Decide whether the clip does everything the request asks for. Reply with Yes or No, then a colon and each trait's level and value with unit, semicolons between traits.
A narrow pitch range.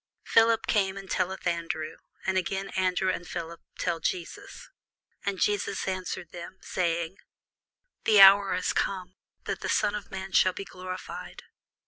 Yes: narrow, 1.8 semitones